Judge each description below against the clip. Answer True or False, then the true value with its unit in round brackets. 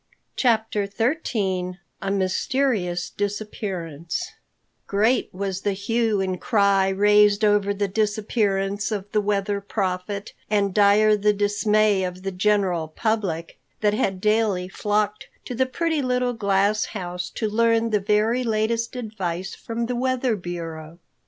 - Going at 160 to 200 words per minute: False (135 wpm)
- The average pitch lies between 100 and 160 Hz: False (205 Hz)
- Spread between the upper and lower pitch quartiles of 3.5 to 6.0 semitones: False (2.4 semitones)